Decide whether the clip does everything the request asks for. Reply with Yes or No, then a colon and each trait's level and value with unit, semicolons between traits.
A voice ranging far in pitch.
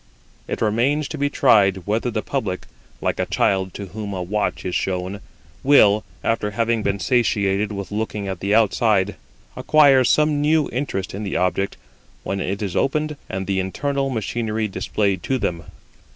No: average, 4.6 semitones